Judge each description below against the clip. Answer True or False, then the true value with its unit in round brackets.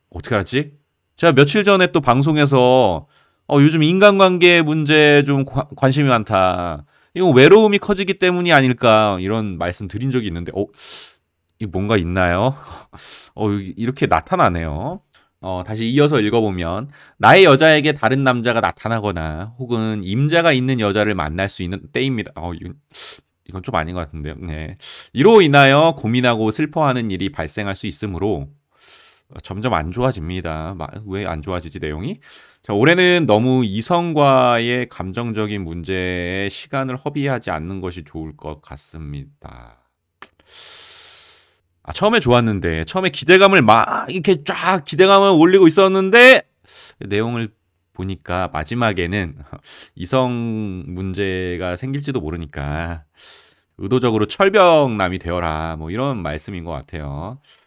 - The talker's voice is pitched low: True (110 Hz)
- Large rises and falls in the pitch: True (7.9 semitones)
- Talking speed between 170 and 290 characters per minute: False (300 characters per minute)